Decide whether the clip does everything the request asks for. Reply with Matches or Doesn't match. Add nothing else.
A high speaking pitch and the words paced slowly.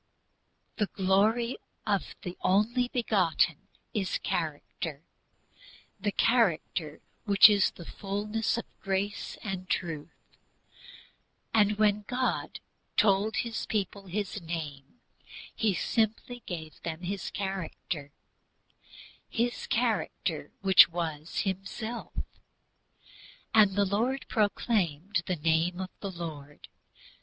Matches